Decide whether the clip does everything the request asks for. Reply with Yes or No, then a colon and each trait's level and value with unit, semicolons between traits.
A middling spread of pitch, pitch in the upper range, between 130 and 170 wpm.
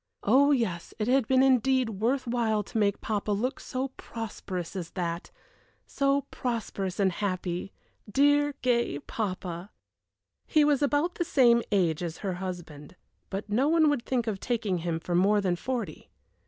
No: wide, 6.0 semitones; high, 215 Hz; average, 160 wpm